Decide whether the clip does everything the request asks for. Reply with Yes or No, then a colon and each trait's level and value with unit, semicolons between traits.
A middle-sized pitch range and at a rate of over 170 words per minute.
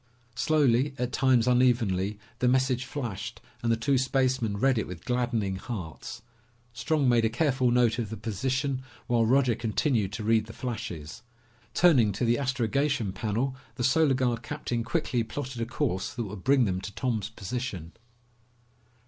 No: average, 3.1 semitones; average, 160 wpm